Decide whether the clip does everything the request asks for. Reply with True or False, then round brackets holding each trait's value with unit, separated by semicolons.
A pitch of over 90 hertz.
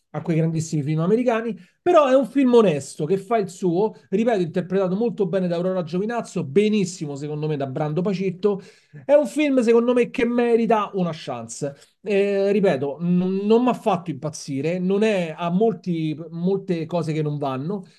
True (190 Hz)